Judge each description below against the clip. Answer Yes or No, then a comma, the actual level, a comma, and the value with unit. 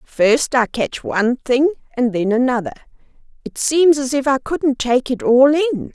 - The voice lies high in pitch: Yes, very high, 260 Hz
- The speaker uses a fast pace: No, average, 180 wpm